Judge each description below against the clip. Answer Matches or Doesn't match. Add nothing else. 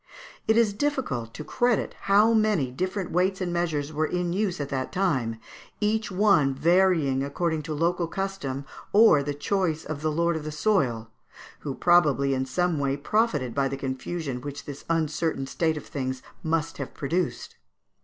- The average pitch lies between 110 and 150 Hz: Doesn't match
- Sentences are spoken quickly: Doesn't match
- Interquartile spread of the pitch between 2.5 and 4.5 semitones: Doesn't match